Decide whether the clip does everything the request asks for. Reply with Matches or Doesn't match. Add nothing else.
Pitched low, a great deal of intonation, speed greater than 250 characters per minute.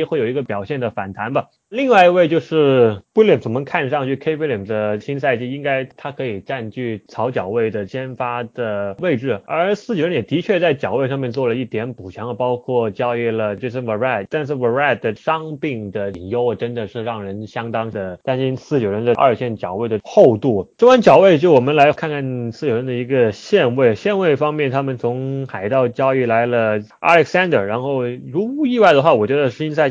Doesn't match